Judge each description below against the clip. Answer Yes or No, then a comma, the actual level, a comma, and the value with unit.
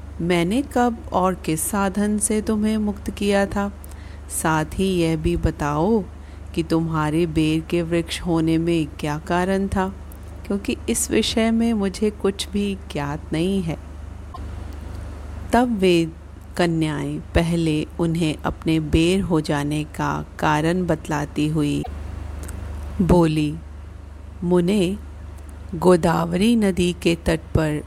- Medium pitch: Yes, medium, 165 Hz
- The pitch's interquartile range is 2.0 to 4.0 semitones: No, average, 4.8 semitones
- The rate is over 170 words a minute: No, average, 120 wpm